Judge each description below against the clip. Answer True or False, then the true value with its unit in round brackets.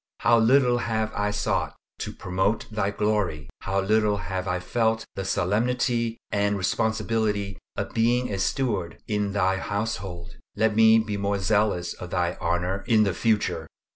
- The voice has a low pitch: True (105 Hz)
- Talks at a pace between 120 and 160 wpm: True (155 wpm)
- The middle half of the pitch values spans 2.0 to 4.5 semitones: True (2.9 semitones)